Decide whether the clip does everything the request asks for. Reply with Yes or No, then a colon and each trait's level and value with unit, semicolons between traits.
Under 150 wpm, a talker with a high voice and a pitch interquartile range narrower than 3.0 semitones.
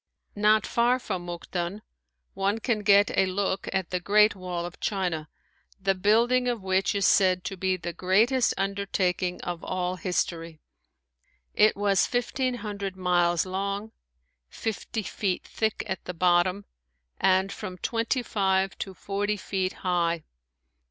Yes: average, 140 wpm; high, 195 Hz; narrow, 2.5 semitones